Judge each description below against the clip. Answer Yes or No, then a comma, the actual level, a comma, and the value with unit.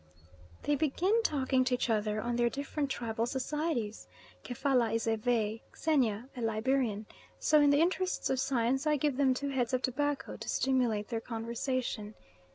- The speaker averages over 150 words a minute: Yes, average, 165 wpm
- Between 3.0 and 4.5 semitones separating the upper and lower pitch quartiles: Yes, average, 3.8 semitones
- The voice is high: Yes, very high, 255 Hz